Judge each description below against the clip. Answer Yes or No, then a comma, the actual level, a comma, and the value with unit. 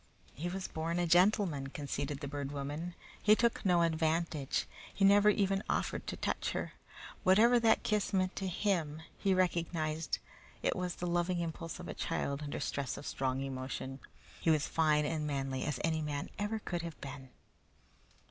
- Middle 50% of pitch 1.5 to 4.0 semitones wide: No, average, 4.4 semitones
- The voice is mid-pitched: Yes, medium, 165 Hz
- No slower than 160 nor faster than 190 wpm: Yes, average, 175 wpm